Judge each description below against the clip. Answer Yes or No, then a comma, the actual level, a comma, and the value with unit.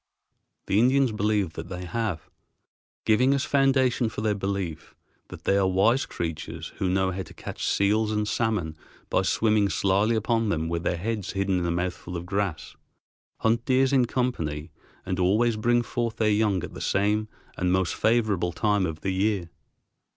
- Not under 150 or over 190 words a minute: Yes, average, 175 wpm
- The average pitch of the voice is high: No, low, 100 Hz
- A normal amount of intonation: Yes, average, 3.8 semitones